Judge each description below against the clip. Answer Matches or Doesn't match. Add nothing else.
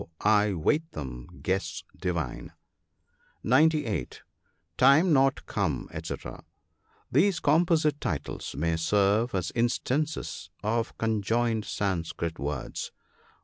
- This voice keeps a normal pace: Doesn't match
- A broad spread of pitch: Matches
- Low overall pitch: Matches